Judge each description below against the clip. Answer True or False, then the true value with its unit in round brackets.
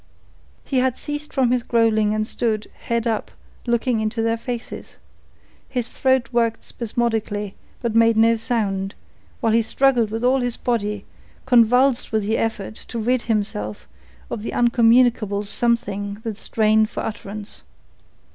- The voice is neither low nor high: False (230 Hz)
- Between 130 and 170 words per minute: True (145 wpm)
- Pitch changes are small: True (2.1 semitones)